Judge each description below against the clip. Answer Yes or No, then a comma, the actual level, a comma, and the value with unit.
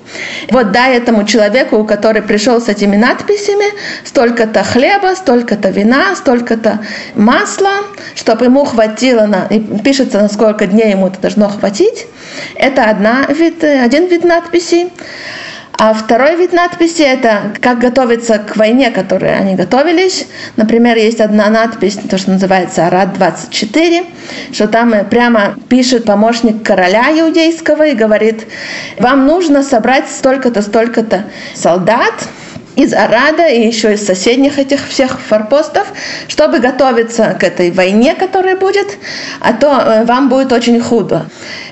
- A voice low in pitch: No, high, 240 Hz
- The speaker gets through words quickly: No, average, 130 wpm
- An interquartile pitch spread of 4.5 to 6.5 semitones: Yes, average, 5.3 semitones